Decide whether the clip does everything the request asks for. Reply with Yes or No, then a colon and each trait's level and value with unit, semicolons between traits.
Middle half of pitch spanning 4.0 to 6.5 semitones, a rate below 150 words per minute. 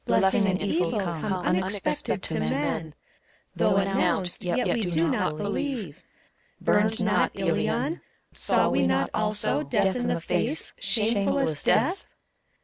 Yes: average, 4.3 semitones; slow, 135 wpm